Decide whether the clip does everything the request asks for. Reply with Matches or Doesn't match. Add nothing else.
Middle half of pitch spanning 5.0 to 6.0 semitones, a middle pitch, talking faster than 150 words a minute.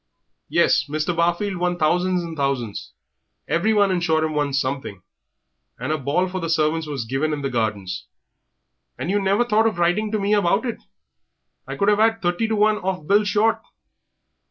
Matches